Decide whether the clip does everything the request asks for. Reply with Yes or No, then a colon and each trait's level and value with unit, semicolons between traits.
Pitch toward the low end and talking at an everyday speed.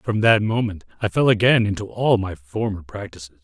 Yes: low, 105 Hz; average, 190 wpm